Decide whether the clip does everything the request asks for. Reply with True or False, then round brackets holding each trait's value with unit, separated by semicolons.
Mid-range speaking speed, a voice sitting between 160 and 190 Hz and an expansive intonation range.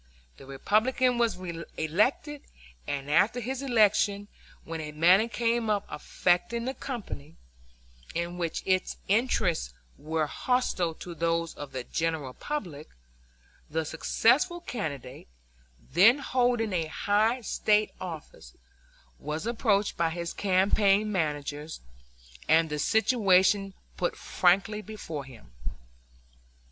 False (110 wpm; 185 Hz; 6.0 semitones)